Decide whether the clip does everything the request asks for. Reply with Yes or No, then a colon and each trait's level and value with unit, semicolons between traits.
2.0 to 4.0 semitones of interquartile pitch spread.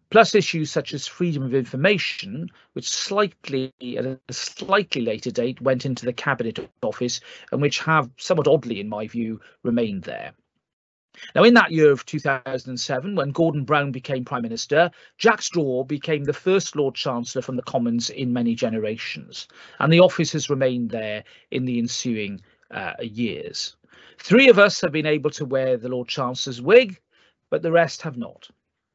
No: average, 5.0 semitones